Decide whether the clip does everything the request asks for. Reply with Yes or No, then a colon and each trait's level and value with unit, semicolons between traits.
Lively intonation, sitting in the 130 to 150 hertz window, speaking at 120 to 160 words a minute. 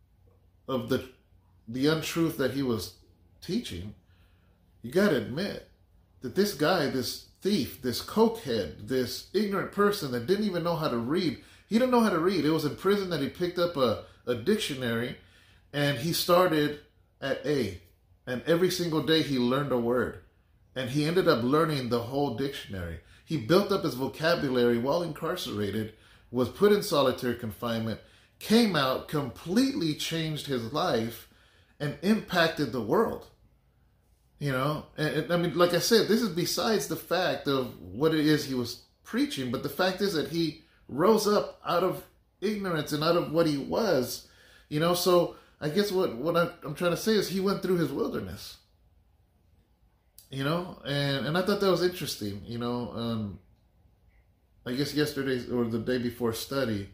No: wide, 7.4 semitones; medium, 140 Hz; average, 170 wpm